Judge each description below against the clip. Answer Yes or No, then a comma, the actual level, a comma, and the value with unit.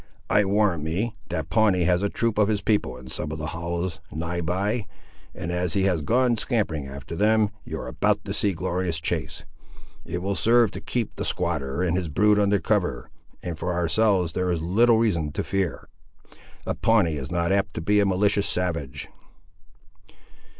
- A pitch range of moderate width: Yes, average, 3.9 semitones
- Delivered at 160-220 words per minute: Yes, average, 190 wpm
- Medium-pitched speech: No, very low, 90 Hz